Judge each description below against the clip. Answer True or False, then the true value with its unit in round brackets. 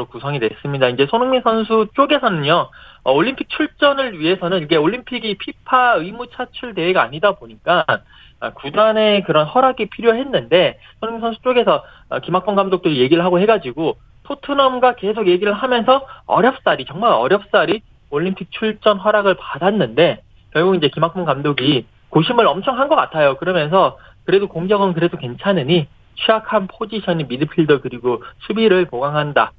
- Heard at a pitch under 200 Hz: False (205 Hz)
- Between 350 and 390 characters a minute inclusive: True (360 characters per minute)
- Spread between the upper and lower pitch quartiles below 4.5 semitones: False (6.3 semitones)